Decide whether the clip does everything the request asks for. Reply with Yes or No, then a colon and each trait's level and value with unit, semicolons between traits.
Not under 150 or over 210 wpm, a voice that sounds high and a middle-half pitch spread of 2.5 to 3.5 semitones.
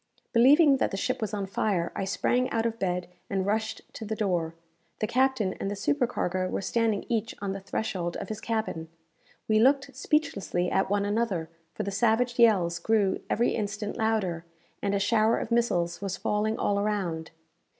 Yes: average, 180 wpm; high, 210 Hz; average, 3.2 semitones